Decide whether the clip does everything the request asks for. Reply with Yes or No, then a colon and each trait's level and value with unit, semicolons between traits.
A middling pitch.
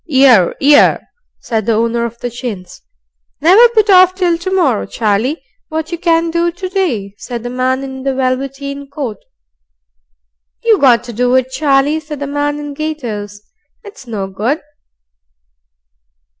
No: very high, 275 Hz